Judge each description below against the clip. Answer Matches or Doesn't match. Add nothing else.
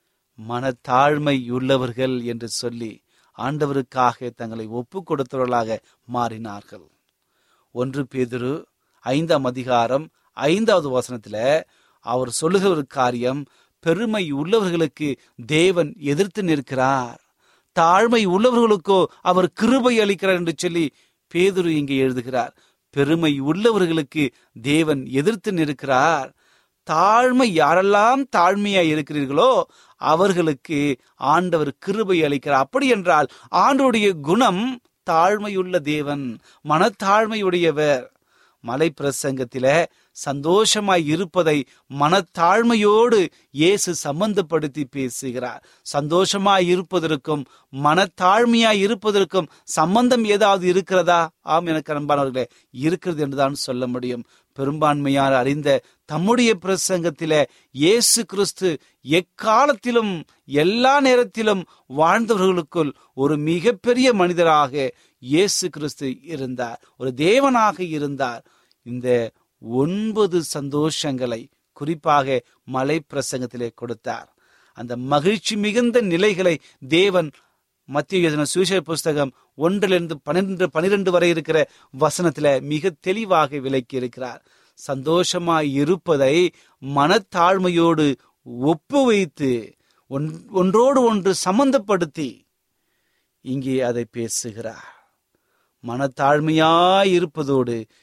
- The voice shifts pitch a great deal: Matches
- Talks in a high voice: Doesn't match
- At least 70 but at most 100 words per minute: Matches